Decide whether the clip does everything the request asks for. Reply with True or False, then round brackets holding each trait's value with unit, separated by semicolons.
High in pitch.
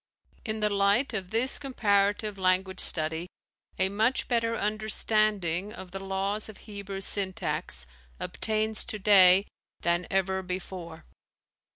True (200 Hz)